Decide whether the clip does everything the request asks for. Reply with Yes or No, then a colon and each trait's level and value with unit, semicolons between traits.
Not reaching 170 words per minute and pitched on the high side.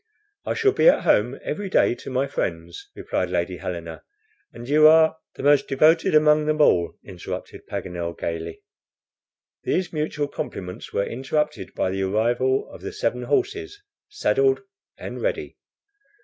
No: average, 150 wpm; medium, 140 Hz